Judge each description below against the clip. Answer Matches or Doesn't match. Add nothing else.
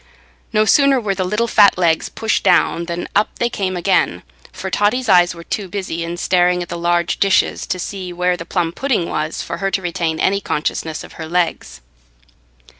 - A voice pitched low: Doesn't match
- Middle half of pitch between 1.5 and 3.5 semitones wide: Matches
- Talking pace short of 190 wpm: Doesn't match